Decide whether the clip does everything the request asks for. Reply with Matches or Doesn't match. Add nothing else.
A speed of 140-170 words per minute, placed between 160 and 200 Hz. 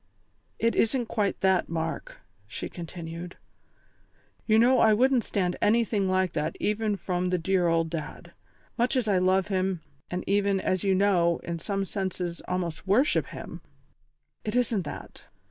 Matches